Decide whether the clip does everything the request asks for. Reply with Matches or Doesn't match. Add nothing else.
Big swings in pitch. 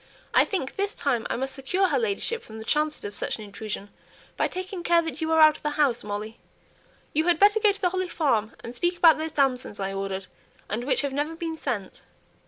Matches